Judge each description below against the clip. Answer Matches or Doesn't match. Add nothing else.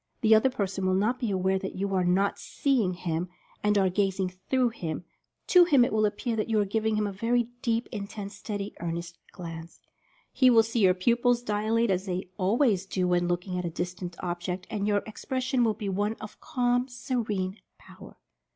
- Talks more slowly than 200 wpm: Doesn't match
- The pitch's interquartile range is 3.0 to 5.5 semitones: Matches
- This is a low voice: Doesn't match